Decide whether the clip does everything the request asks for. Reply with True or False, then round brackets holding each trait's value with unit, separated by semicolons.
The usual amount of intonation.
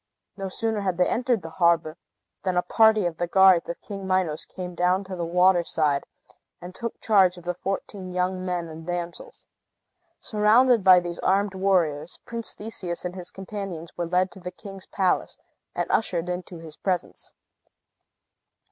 False (2.0 semitones)